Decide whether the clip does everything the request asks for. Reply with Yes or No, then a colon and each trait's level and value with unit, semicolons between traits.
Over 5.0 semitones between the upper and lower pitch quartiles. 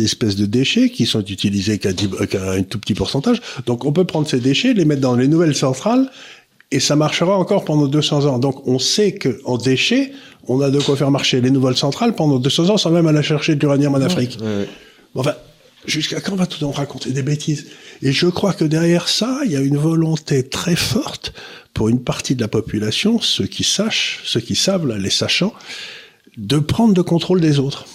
Yes: wide, 5.5 semitones